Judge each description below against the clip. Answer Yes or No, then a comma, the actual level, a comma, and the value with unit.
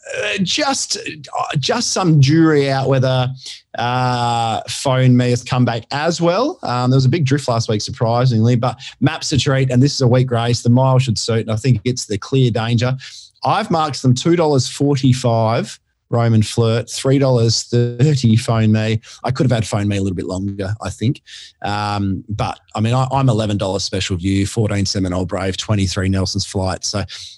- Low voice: Yes, low, 120 Hz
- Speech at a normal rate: Yes, average, 195 wpm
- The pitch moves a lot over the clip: No, average, 3.7 semitones